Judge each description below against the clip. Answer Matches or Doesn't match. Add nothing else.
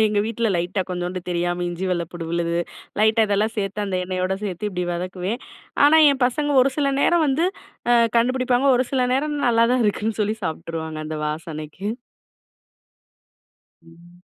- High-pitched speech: Matches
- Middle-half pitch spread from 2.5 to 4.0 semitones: Doesn't match